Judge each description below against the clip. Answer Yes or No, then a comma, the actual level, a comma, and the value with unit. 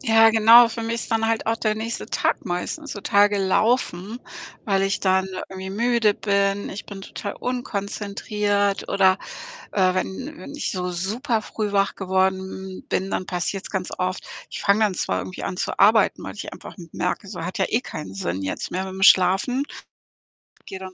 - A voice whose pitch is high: Yes, high, 200 Hz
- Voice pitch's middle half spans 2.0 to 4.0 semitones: Yes, average, 2.9 semitones